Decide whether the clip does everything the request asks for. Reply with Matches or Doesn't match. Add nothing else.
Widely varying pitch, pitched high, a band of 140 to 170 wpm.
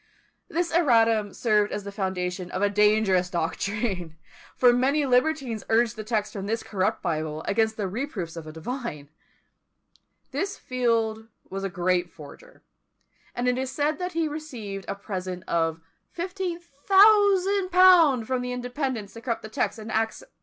Matches